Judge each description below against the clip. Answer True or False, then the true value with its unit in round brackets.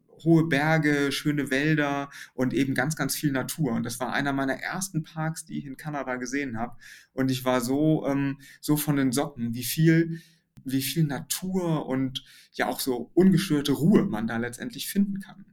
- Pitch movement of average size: True (3.5 semitones)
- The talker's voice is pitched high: False (140 Hz)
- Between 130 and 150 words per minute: False (185 wpm)